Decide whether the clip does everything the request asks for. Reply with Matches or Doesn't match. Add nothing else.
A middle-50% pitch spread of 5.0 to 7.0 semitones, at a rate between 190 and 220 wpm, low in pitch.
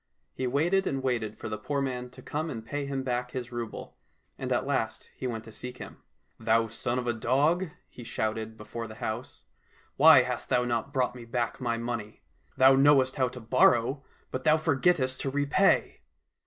Doesn't match